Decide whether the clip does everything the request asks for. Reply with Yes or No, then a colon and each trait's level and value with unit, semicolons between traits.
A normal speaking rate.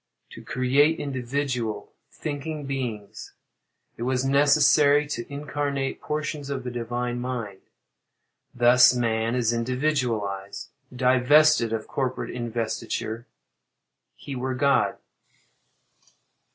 No: slow, 95 wpm